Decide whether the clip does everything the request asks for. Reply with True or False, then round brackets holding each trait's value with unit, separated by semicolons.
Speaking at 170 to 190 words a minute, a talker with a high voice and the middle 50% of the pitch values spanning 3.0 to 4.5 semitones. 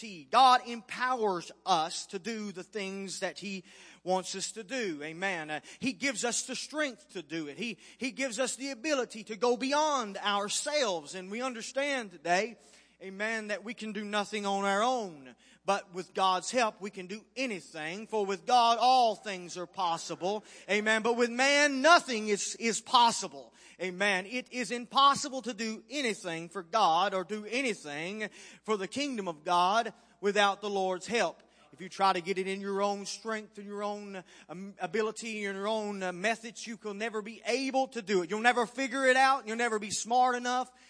True (185 wpm; 215 Hz; 4.1 semitones)